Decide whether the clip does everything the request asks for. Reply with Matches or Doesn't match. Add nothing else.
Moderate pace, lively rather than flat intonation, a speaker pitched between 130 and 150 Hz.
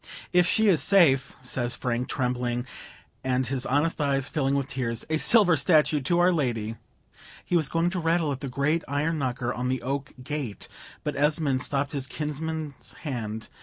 Doesn't match